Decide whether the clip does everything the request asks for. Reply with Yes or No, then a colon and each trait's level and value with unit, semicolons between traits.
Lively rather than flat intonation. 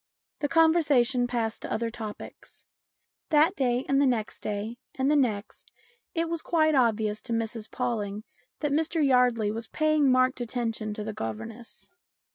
No: average, 4.7 semitones